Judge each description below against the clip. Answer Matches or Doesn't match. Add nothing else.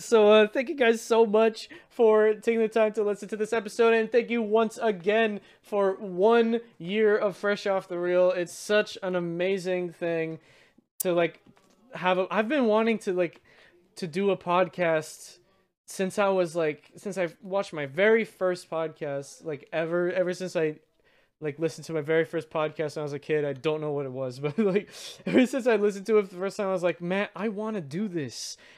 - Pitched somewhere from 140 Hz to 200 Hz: Matches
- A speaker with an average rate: Doesn't match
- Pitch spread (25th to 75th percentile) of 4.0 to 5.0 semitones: Matches